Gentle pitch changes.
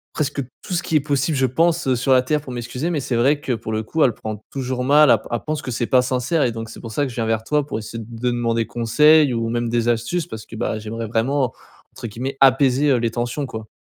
No: average, 3.7 semitones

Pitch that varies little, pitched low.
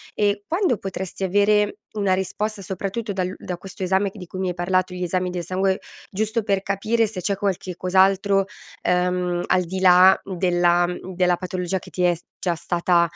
No: narrow, 1.8 semitones; medium, 185 Hz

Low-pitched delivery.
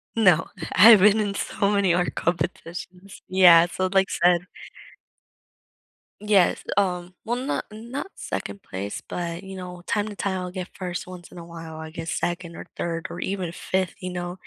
No: medium, 180 Hz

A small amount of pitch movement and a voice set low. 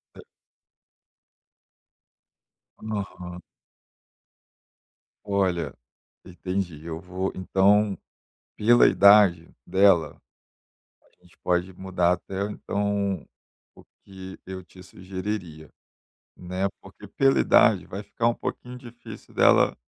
Yes: narrow, 2.2 semitones; very low, 95 Hz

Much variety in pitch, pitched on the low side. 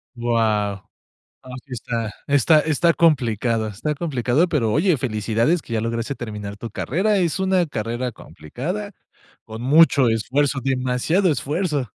Yes: wide, 5.7 semitones; low, 130 Hz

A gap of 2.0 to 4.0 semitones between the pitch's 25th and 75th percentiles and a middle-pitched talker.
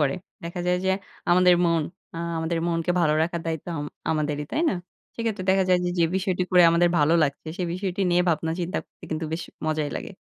Yes: narrow, 2.4 semitones; medium, 170 Hz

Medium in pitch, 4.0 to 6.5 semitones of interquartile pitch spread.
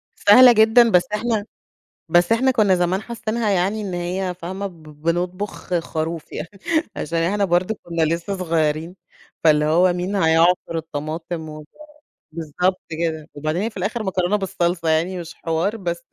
No: medium, 175 Hz; average, 3.4 semitones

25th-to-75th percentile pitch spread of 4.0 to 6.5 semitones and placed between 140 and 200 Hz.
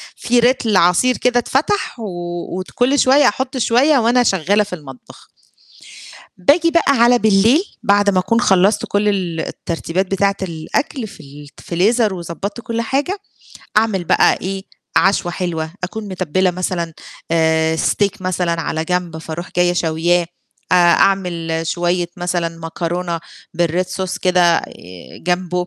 Yes: average, 4.3 semitones; medium, 185 Hz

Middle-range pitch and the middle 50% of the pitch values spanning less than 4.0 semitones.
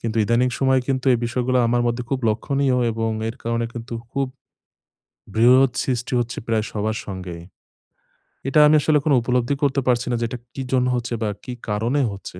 No: low, 120 Hz; narrow, 2.5 semitones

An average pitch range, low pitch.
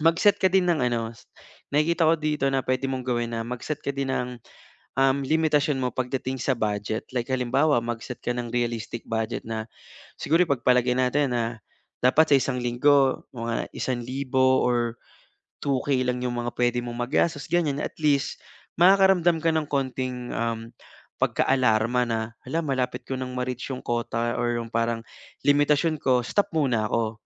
Yes: average, 3.2 semitones; low, 125 Hz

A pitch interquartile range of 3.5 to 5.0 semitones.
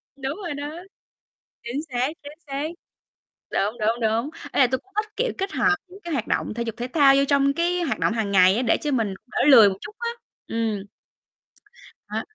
No: wide, 5.4 semitones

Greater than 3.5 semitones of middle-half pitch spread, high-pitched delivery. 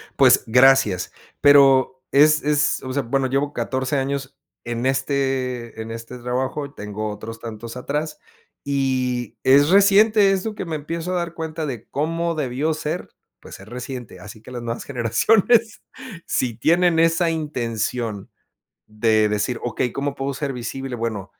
No: average, 4.5 semitones; low, 135 Hz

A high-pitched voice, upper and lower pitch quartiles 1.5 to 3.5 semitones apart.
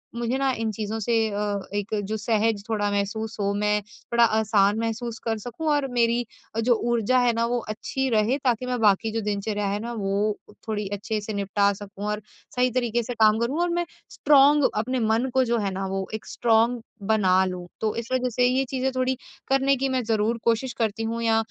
Yes: high, 225 Hz; average, 2.8 semitones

